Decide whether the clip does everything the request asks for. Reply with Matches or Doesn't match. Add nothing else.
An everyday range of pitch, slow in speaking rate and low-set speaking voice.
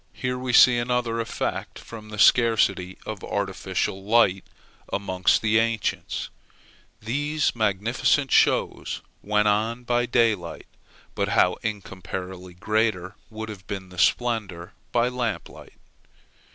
Matches